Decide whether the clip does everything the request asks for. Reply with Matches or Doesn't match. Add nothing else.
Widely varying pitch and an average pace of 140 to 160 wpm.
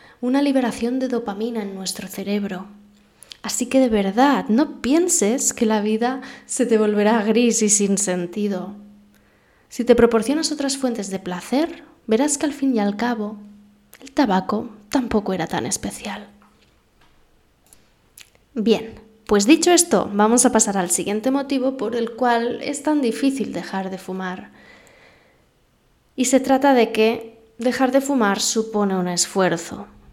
Doesn't match